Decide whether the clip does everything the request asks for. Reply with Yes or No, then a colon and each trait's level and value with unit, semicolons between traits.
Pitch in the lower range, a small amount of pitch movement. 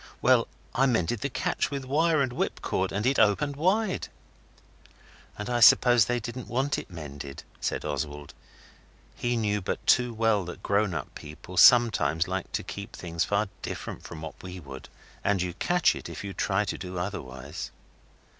No: low, 105 Hz; wide, 5.6 semitones